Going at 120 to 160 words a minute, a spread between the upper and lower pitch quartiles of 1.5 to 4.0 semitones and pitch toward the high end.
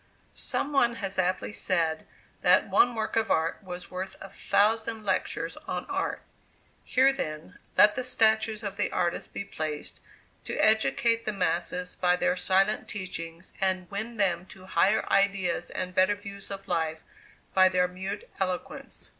Yes: average, 155 wpm; average, 3.1 semitones; high, 195 Hz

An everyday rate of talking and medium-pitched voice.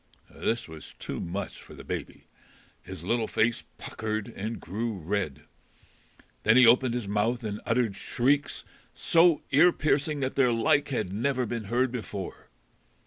No: average, 150 wpm; low, 115 Hz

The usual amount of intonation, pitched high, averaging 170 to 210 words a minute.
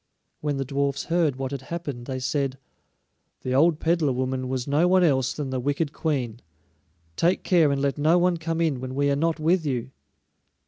No: average, 3.8 semitones; medium, 140 Hz; average, 195 wpm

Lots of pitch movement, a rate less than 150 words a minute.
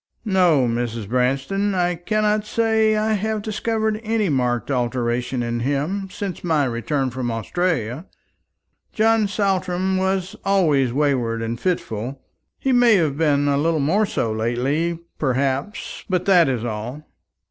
Yes: wide, 7.8 semitones; average, 140 wpm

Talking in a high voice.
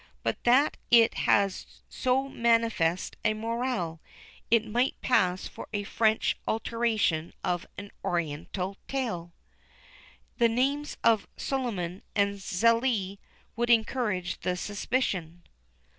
Yes: high, 220 Hz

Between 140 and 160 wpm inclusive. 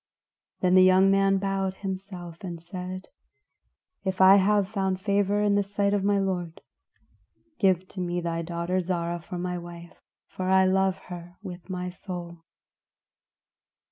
Yes: average, 150 wpm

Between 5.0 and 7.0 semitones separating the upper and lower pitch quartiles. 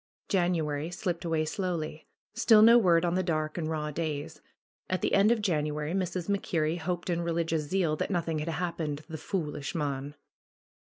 No: average, 2.8 semitones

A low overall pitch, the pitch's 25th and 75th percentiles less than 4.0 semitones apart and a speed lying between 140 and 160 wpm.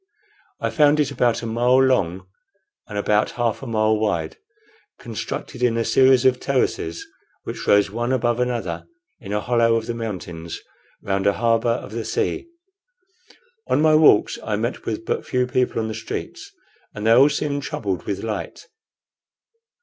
No: low, 115 Hz; average, 3.3 semitones; average, 170 wpm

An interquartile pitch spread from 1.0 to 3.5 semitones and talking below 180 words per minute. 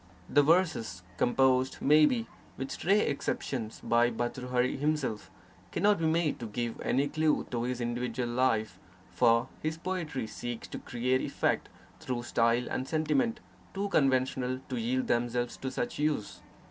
No: average, 4.6 semitones; average, 160 wpm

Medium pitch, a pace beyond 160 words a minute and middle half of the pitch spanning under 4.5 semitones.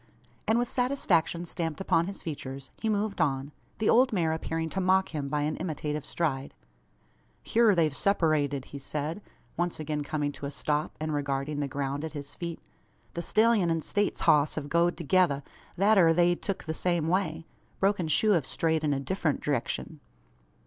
Yes: medium, 160 Hz; average, 180 wpm; average, 4.1 semitones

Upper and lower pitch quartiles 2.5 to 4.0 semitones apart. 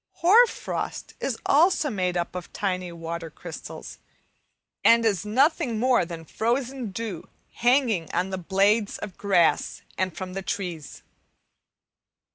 No: average, 5.2 semitones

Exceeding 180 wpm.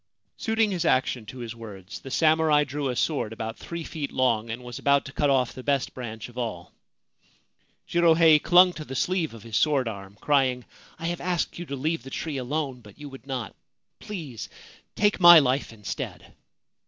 Yes: average, 195 wpm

